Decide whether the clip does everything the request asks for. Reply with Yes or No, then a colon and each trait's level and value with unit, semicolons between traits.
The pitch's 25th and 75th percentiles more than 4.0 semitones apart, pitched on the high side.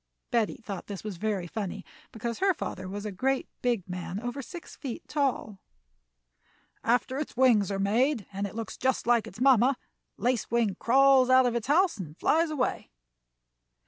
Yes: average, 4.5 semitones; high, 235 Hz